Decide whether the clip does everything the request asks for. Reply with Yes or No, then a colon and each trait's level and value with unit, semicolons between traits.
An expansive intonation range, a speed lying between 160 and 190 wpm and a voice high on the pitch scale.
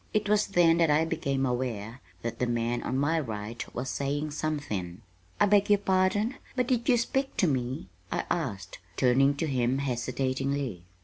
No: wide, 6.2 semitones; average, 175 wpm; medium, 140 Hz